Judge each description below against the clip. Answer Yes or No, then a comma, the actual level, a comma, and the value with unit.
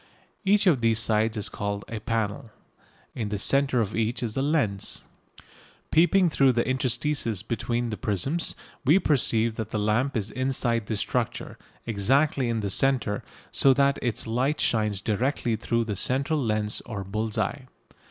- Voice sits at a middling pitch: No, low, 115 Hz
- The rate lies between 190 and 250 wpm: No, average, 160 wpm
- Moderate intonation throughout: Yes, average, 3.9 semitones